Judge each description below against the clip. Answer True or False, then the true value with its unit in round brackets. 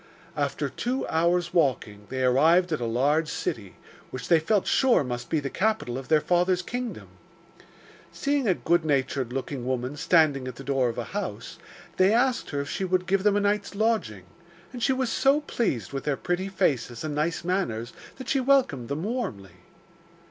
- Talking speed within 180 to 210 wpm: True (185 wpm)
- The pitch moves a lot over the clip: True (7.5 semitones)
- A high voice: False (160 Hz)